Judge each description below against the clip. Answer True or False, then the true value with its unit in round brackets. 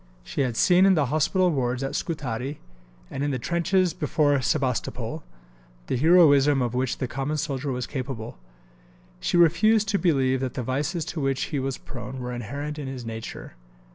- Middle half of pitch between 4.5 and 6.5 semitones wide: False (3.8 semitones)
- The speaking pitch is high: False (140 Hz)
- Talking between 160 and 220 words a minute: True (175 wpm)